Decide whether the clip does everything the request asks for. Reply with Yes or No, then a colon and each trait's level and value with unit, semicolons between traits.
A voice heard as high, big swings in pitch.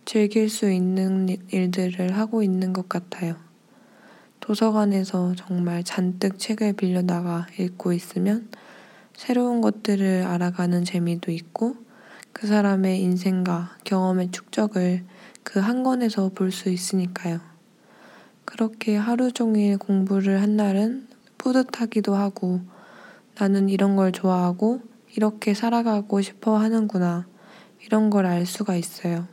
No: high, 195 Hz; average, 3.1 semitones